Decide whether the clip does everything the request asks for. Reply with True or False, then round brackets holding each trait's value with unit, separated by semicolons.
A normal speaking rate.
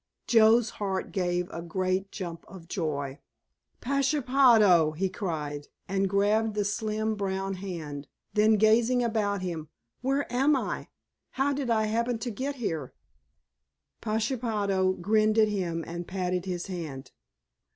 False (130 wpm)